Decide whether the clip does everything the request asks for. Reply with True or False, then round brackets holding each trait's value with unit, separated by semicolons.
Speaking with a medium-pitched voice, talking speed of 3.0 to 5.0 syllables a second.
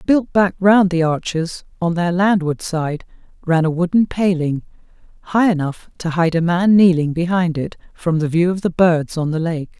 True (170 Hz; 4.7 syllables/s)